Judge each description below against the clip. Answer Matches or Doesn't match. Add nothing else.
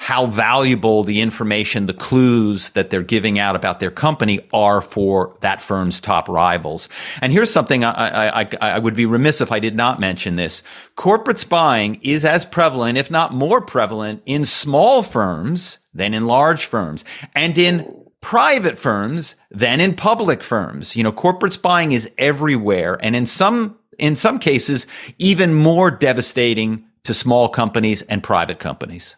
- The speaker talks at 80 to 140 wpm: Doesn't match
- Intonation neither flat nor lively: Doesn't match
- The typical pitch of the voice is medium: Doesn't match